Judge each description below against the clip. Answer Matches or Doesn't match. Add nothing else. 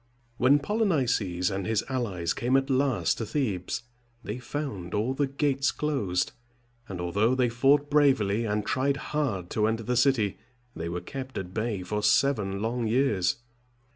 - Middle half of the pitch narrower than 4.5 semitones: Doesn't match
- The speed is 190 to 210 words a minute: Doesn't match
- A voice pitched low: Matches